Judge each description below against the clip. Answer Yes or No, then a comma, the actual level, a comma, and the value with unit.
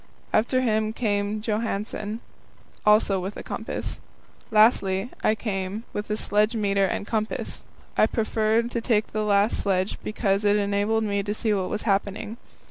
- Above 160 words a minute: No, average, 150 wpm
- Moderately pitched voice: No, high, 210 Hz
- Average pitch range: No, narrow, 1.5 semitones